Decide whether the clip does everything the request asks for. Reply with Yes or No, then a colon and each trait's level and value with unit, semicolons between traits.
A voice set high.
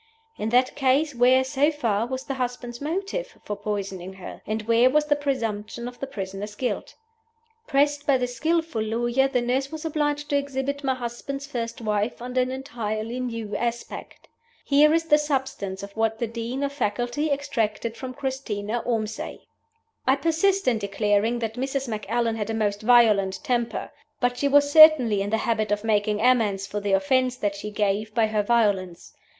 Yes: high, 240 Hz